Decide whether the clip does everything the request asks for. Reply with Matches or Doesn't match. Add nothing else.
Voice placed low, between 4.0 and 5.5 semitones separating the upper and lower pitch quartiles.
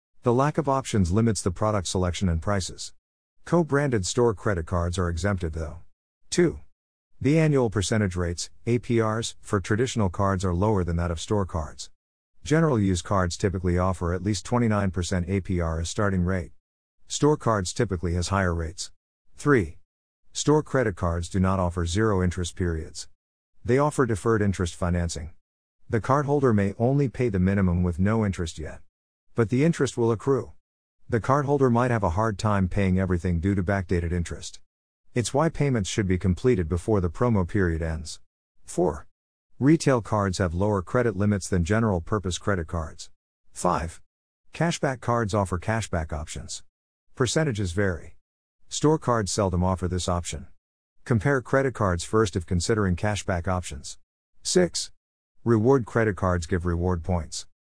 Matches